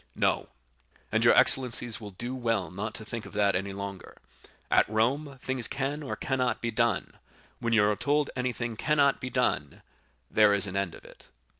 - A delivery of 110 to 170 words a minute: No, average, 185 wpm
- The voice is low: Yes, low, 115 Hz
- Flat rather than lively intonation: No, average, 3.9 semitones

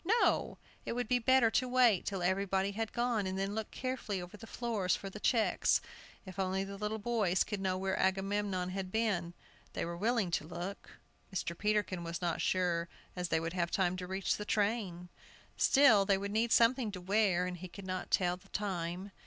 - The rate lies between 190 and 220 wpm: Yes, average, 200 wpm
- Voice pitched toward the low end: No, high, 195 Hz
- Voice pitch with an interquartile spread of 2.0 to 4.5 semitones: Yes, average, 3.0 semitones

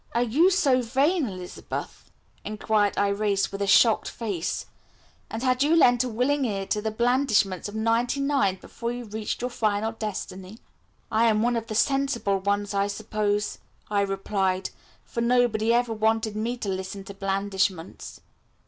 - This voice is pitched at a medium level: No, high, 220 Hz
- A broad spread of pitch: No, average, 3.4 semitones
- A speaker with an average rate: Yes, average, 160 wpm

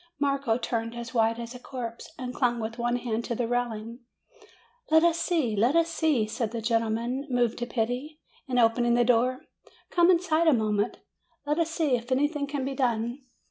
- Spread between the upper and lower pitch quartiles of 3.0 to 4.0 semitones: Yes, average, 3.6 semitones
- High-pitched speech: Yes, high, 245 Hz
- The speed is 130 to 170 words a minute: No, average, 195 wpm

